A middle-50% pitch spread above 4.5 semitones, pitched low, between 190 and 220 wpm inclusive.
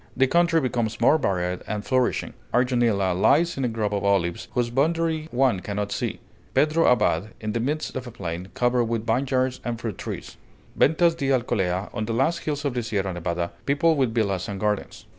Yes: average, 5.0 semitones; low, 120 Hz; average, 195 wpm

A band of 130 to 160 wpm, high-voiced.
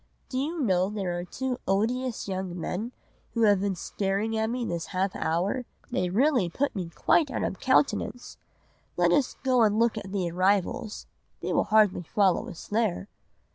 No: average, 175 wpm; high, 205 Hz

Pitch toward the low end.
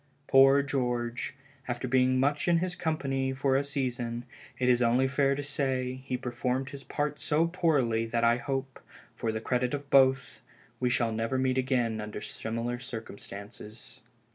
Yes: low, 130 Hz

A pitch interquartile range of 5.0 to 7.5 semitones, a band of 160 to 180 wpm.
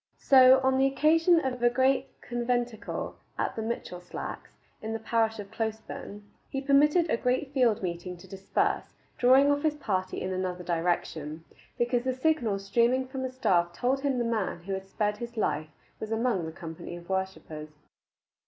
Yes: wide, 5.5 semitones; average, 170 wpm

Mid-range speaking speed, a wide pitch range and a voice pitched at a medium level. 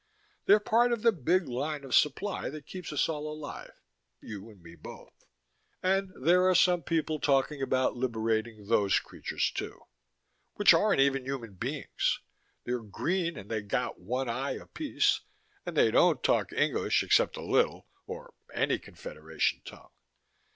Yes: average, 155 wpm; wide, 7.5 semitones; medium, 145 Hz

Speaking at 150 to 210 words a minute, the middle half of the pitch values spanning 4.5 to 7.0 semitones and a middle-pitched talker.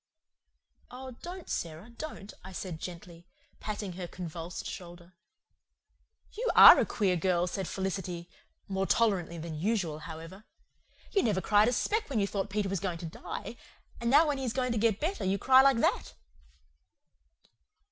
No: average, 165 wpm; average, 5.2 semitones; high, 195 Hz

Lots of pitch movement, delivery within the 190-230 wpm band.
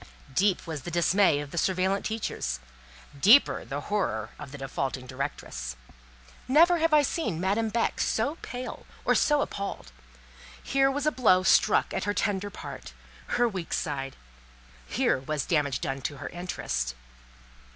No: wide, 8.6 semitones; average, 150 wpm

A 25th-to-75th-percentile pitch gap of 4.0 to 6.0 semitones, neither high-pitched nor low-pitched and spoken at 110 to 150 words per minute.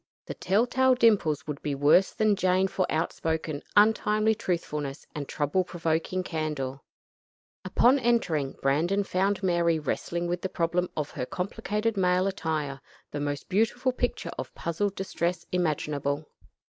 Yes: average, 4.7 semitones; medium, 175 Hz; average, 140 wpm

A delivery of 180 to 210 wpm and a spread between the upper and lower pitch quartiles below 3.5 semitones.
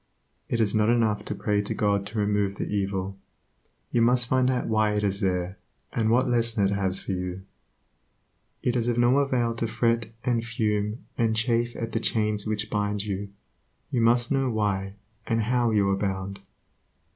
Yes: average, 185 wpm; average, 2.7 semitones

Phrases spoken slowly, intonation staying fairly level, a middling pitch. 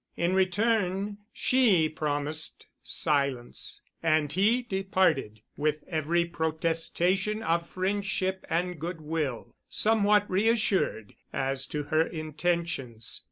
No: slow, 100 wpm; average, 3.9 semitones; medium, 170 Hz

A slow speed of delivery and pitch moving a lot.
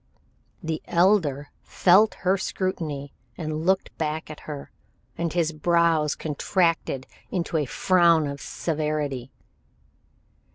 No: slow, 110 wpm; average, 2.7 semitones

